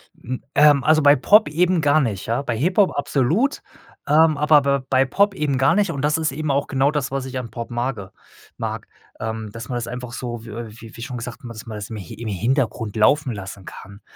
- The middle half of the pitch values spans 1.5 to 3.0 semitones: No, average, 4.5 semitones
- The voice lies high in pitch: No, low, 130 Hz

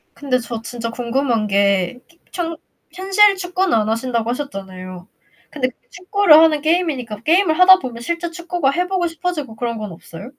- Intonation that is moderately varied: No, wide, 7.4 semitones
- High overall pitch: Yes, very high, 275 Hz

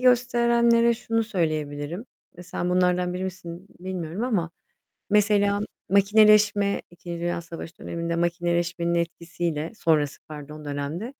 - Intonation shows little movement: No, average, 3.8 semitones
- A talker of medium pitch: Yes, medium, 175 Hz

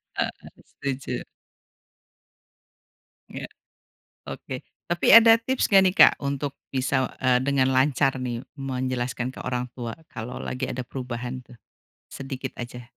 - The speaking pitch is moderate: No, low, 130 Hz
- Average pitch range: No, narrow, 1.9 semitones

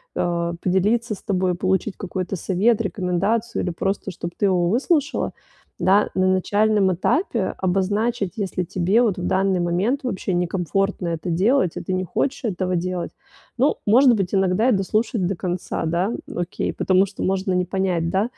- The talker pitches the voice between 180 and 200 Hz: Yes, high, 190 Hz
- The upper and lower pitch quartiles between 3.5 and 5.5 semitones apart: No, average, 2.8 semitones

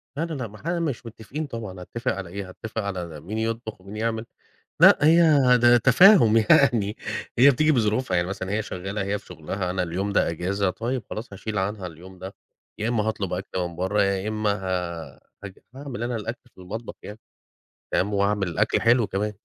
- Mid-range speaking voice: No, low, 105 Hz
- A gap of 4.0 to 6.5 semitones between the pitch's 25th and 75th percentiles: No, average, 3.6 semitones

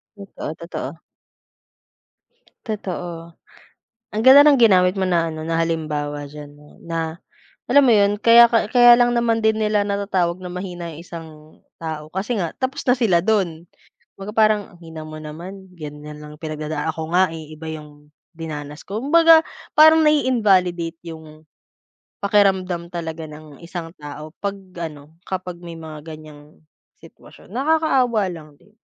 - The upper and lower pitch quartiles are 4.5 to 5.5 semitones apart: Yes, average, 5.2 semitones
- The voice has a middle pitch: Yes, medium, 170 Hz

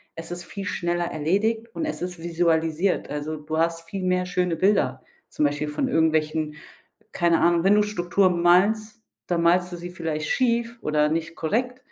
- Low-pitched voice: No, medium, 175 Hz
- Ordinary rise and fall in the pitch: Yes, average, 3.4 semitones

